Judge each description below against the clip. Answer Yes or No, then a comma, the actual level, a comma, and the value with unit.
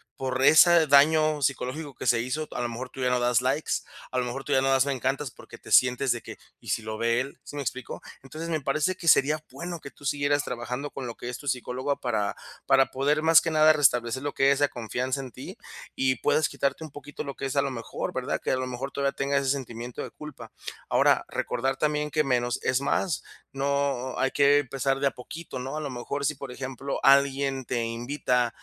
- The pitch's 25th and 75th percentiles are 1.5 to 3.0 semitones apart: Yes, narrow, 2.4 semitones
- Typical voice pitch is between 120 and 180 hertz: Yes, low, 135 Hz